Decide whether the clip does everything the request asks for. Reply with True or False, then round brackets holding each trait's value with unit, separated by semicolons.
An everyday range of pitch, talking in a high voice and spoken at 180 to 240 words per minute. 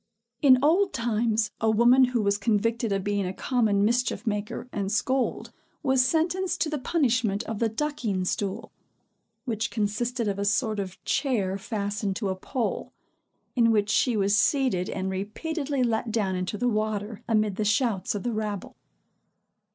False (3.5 semitones; 220 Hz; 165 wpm)